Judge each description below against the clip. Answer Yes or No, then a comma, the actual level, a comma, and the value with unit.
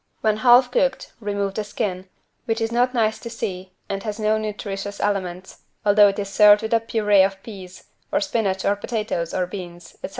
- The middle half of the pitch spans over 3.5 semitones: No, narrow, 2.5 semitones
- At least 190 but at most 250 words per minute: Yes, average, 195 wpm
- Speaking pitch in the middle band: No, high, 205 Hz